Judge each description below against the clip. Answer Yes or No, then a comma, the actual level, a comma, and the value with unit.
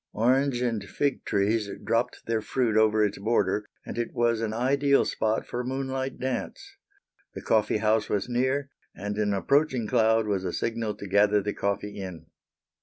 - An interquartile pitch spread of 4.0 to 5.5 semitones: No, average, 3.4 semitones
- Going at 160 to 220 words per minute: Yes, average, 175 wpm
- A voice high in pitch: No, low, 110 Hz